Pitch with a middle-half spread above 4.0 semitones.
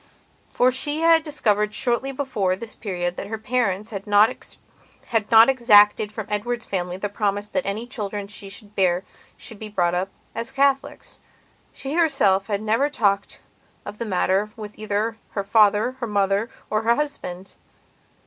No: average, 3.2 semitones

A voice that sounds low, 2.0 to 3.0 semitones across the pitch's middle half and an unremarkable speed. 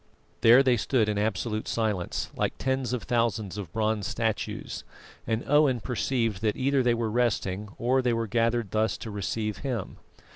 Yes: low, 115 Hz; narrow, 2.4 semitones; average, 175 wpm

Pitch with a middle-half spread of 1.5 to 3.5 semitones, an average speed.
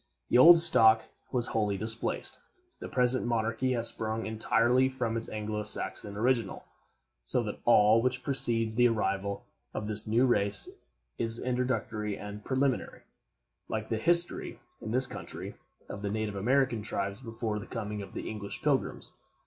Yes: average, 2.9 semitones; average, 155 wpm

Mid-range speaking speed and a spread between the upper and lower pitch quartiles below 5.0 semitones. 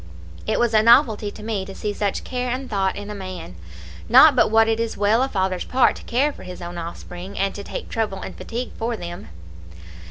No: fast, 225 wpm; average, 3.7 semitones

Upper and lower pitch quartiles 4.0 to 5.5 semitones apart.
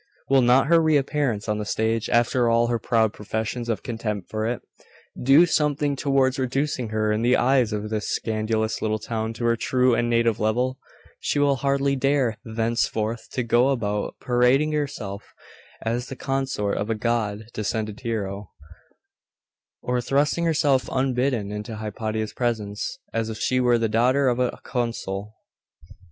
No: average, 3.4 semitones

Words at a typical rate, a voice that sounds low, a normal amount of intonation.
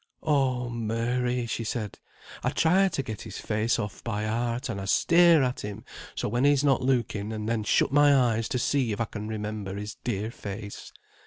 Yes: average, 195 wpm; low, 115 Hz; average, 3.3 semitones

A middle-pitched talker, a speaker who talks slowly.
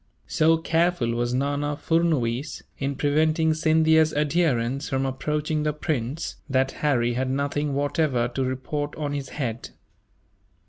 Yes: medium, 145 Hz; slow, 130 wpm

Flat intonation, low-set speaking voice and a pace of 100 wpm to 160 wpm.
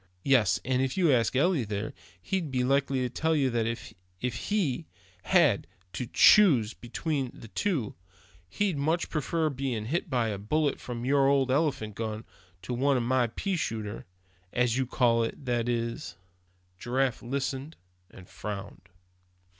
No: average, 3.5 semitones; low, 130 Hz; average, 155 wpm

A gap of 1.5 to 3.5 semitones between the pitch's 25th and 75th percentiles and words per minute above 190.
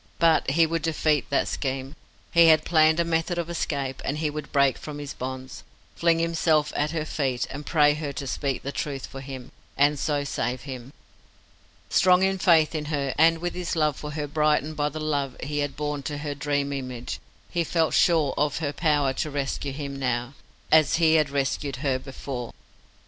Yes: narrow, 2.4 semitones; average, 200 wpm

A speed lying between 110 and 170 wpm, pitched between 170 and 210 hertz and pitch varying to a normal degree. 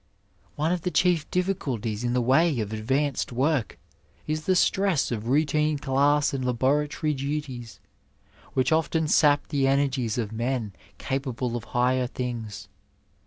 No: average, 140 wpm; low, 135 Hz; average, 3.9 semitones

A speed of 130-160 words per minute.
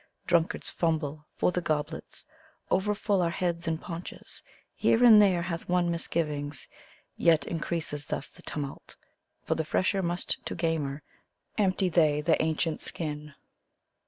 Yes: average, 140 wpm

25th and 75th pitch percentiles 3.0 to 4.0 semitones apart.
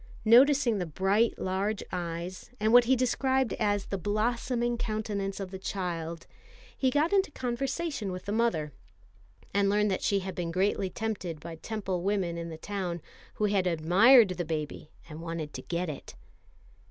No: average, 4.7 semitones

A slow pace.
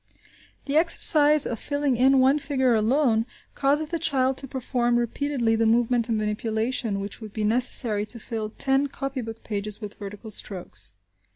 No: average, 165 wpm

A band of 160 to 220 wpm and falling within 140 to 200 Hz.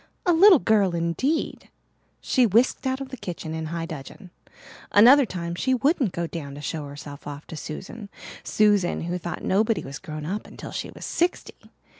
Yes: average, 180 wpm; medium, 185 Hz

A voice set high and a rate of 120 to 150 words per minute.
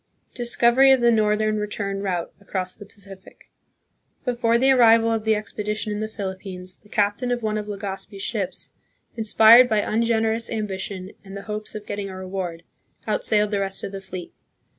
No: high, 210 Hz; average, 175 wpm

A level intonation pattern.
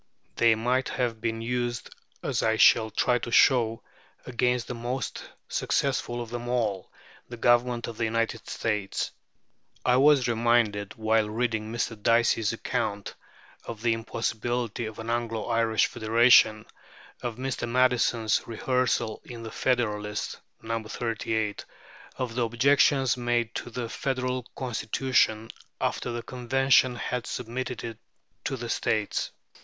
Yes: narrow, 1.8 semitones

